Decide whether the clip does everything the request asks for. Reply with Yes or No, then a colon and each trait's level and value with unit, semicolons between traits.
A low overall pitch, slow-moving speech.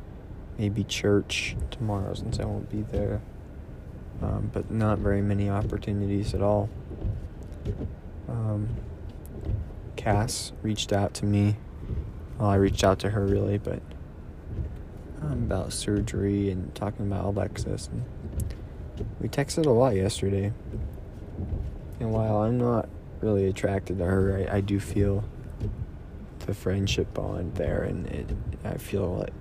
Yes: low, 100 Hz; slow, 130 wpm